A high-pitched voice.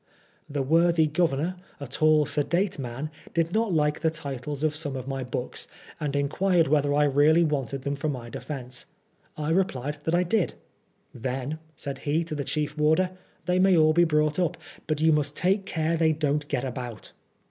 No: medium, 150 Hz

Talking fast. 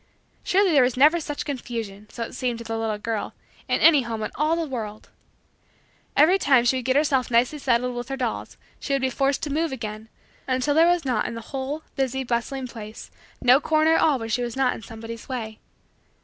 Yes: fast, 220 wpm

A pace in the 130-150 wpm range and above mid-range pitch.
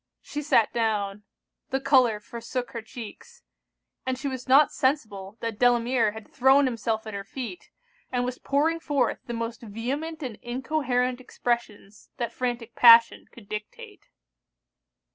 Yes: average, 145 wpm; high, 245 Hz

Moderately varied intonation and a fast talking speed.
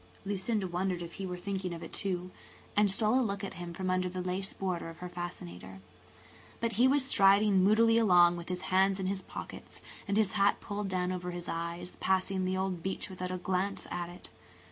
No: narrow, 1.9 semitones; fast, 210 wpm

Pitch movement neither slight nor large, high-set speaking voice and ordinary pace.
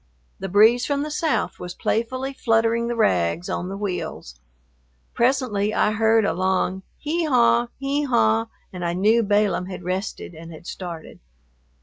Yes: average, 4.9 semitones; high, 210 Hz; average, 155 wpm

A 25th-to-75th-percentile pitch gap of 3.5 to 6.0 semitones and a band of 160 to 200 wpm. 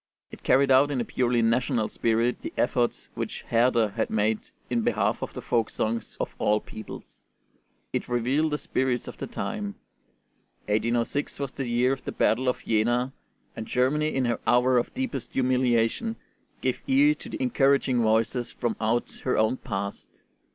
No: average, 2.8 semitones; average, 170 wpm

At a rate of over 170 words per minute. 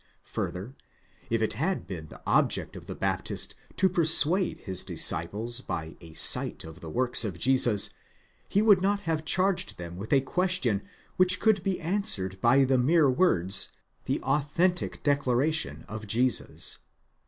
No: average, 155 wpm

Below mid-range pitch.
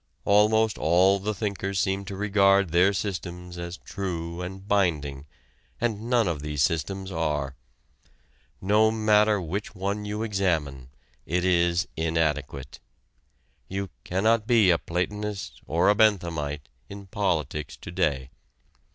Yes: very low, 95 Hz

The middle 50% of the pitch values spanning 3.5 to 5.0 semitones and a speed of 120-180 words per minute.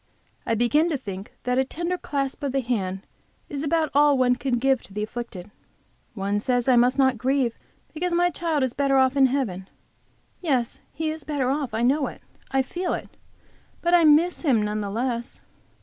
No: average, 3.9 semitones; average, 195 wpm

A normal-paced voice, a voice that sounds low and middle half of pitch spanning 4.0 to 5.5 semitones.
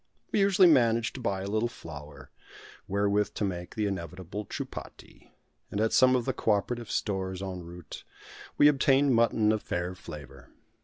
Yes: average, 165 wpm; low, 105 Hz; average, 4.5 semitones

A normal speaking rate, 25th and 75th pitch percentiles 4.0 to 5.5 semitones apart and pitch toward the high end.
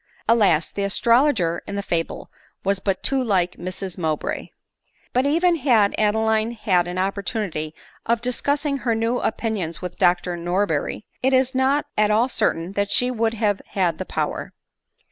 Yes: average, 165 wpm; average, 4.9 semitones; high, 210 Hz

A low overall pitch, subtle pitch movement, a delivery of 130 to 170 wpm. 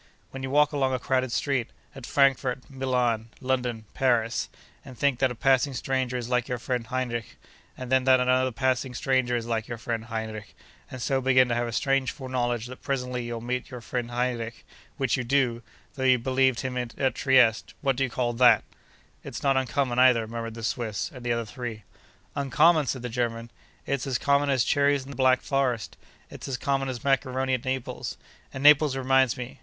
No: low, 125 Hz; narrow, 1.9 semitones; average, 190 wpm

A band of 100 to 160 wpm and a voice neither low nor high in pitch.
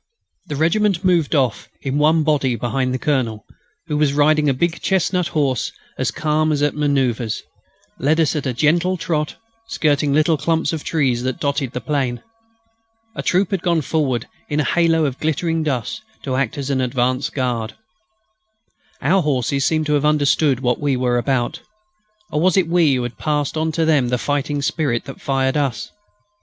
No: average, 185 wpm; medium, 145 Hz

